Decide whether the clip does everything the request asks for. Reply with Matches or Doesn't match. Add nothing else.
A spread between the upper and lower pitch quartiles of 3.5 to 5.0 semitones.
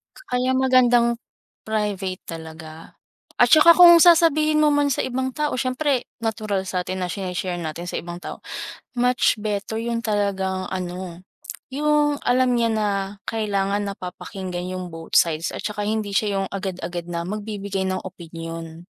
Doesn't match